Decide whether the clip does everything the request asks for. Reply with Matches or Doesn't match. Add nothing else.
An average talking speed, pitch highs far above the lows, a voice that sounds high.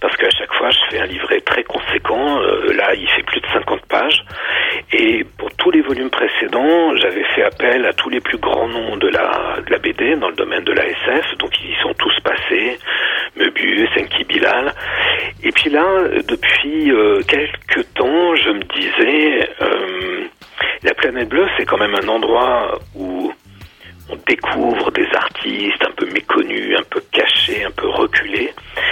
Matches